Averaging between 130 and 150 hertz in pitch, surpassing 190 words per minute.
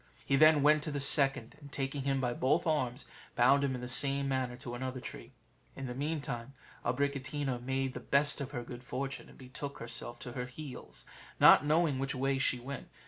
Yes: low, 135 Hz; average, 200 wpm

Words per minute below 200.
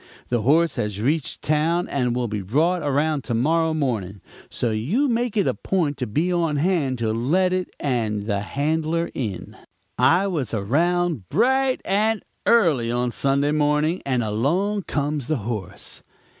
Yes: average, 160 wpm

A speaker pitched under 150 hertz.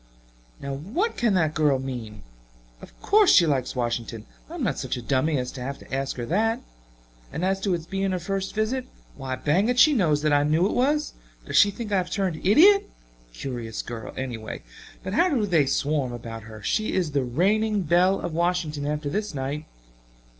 No: medium, 160 Hz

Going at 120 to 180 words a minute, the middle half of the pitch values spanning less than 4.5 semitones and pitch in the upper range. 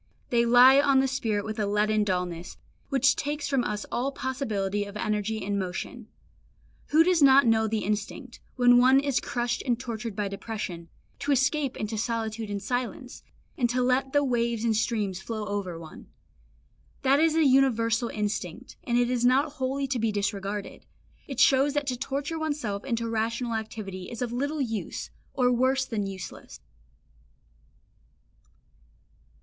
Yes: average, 160 wpm; average, 4.0 semitones; high, 235 Hz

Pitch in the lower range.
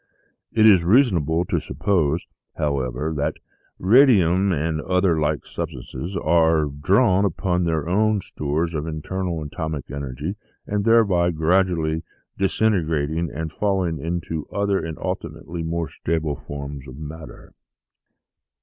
Yes: very low, 80 Hz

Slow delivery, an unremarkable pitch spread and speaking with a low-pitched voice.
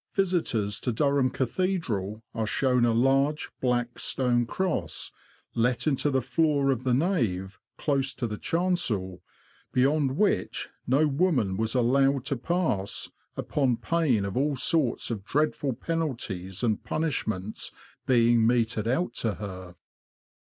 Yes: slow, 130 wpm; average, 4.9 semitones; low, 125 Hz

